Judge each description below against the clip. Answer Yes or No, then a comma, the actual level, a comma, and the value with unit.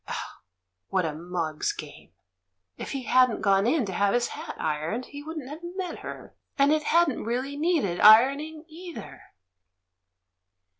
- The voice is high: Yes, very high, 255 Hz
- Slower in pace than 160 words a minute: Yes, average, 150 wpm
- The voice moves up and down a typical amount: No, wide, 7.8 semitones